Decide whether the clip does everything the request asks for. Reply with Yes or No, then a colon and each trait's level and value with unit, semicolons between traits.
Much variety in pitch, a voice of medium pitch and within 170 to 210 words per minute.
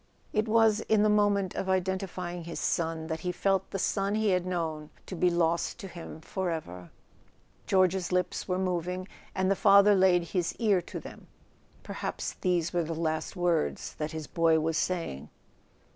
No: narrow, 2.6 semitones; medium, 180 Hz; average, 175 wpm